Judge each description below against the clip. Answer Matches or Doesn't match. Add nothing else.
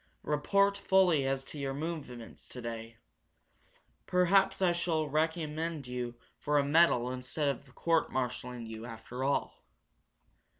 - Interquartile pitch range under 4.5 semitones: Doesn't match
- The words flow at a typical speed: Doesn't match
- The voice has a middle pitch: Matches